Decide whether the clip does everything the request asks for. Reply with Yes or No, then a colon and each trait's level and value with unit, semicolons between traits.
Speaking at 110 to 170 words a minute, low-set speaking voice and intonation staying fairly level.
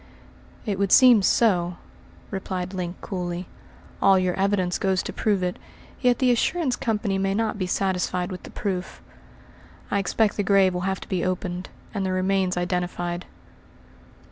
No: average, 160 wpm; high, 190 Hz; narrow, 2.0 semitones